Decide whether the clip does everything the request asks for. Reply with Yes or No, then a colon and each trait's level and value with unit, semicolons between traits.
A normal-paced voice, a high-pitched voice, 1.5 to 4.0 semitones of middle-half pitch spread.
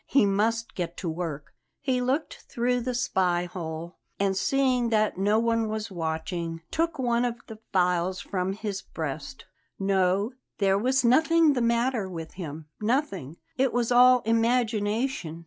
No: average, 150 wpm; high, 215 Hz; wide, 5.5 semitones